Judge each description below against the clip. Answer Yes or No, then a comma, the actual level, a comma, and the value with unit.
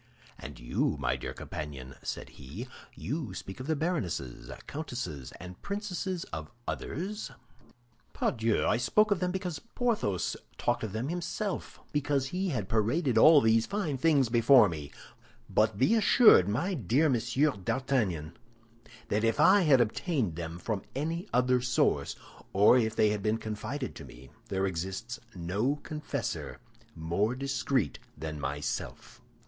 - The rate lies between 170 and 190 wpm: No, average, 145 wpm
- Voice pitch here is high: No, low, 120 Hz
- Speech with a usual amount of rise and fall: No, wide, 8.2 semitones